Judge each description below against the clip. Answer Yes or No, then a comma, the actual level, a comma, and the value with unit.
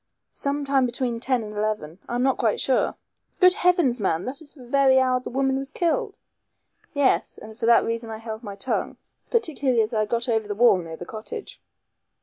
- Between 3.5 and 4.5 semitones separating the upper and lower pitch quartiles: Yes, average, 3.9 semitones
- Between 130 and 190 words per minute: No, average, 200 wpm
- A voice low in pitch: No, high, 245 Hz